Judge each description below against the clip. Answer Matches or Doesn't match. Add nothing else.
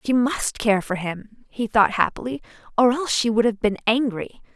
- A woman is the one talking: Matches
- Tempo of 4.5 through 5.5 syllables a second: Matches